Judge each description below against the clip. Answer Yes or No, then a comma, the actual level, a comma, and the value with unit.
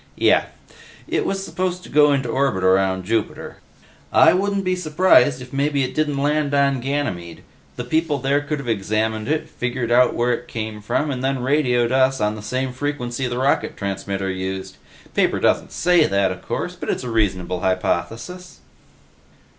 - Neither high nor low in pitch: No, low, 130 Hz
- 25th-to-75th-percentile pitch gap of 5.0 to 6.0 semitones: Yes, wide, 5.4 semitones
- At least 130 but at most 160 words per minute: No, average, 175 wpm